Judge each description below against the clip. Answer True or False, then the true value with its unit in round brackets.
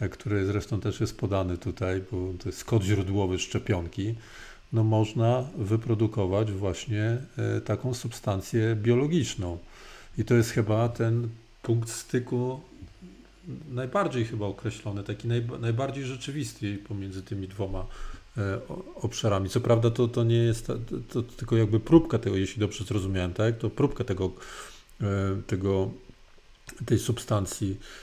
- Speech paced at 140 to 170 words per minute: False (125 wpm)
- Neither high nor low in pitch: False (110 Hz)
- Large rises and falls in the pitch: False (3.3 semitones)